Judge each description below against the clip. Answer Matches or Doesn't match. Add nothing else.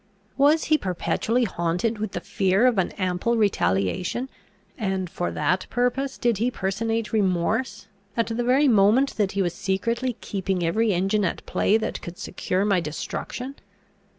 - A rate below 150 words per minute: Doesn't match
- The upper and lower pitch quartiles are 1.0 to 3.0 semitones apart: Doesn't match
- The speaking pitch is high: Matches